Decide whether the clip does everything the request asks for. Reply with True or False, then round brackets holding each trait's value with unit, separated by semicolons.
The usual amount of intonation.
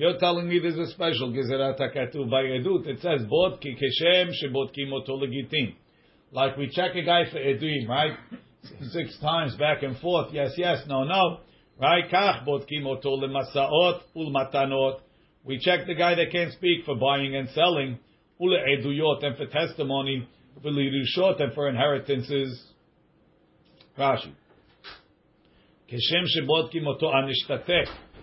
True (4.0 semitones)